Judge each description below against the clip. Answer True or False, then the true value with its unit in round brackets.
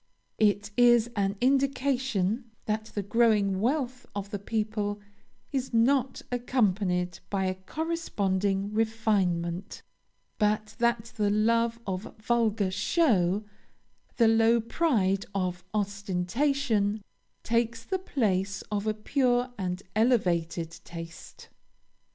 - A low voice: False (215 Hz)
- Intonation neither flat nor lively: True (3.5 semitones)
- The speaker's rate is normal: False (105 wpm)